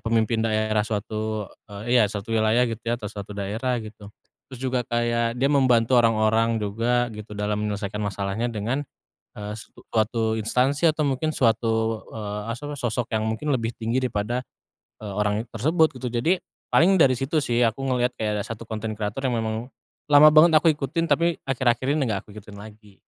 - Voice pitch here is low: Yes, low, 115 Hz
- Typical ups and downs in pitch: Yes, average, 3.0 semitones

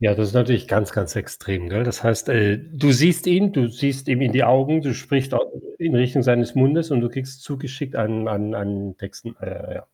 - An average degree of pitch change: Yes, average, 3.9 semitones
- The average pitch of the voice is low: Yes, low, 125 Hz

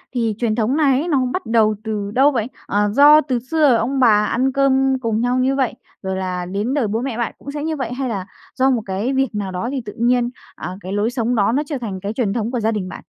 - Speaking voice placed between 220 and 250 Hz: Yes, high, 240 Hz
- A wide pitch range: No, average, 4.1 semitones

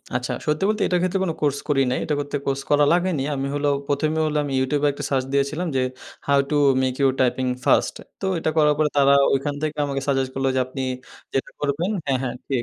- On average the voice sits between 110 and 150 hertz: Yes, medium, 140 Hz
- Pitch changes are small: Yes, narrow, 2.0 semitones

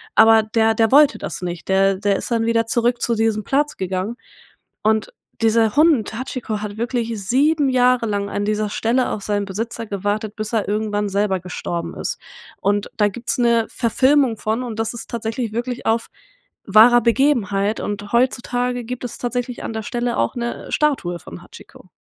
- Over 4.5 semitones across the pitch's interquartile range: No, average, 2.8 semitones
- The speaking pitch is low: No, high, 225 Hz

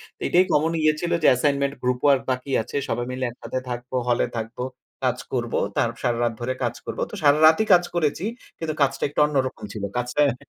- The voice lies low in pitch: Yes, low, 130 Hz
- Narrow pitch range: No, average, 3.4 semitones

